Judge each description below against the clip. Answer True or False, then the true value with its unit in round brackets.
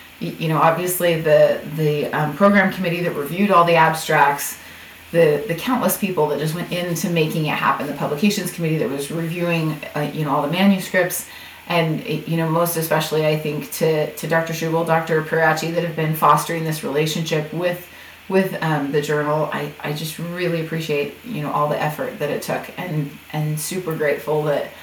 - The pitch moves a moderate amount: False (2.2 semitones)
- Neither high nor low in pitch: True (160 Hz)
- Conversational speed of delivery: True (190 wpm)